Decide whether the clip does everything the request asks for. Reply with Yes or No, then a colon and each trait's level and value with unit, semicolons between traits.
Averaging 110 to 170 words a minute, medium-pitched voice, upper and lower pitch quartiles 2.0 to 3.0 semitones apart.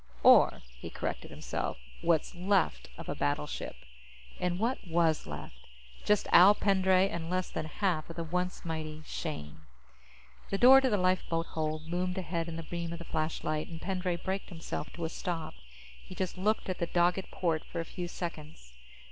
No: average, 180 wpm; medium, 170 Hz; narrow, 2.5 semitones